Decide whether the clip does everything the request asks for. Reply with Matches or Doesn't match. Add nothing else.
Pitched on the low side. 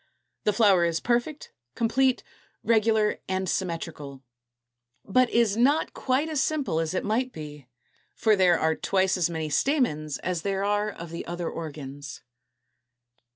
Doesn't match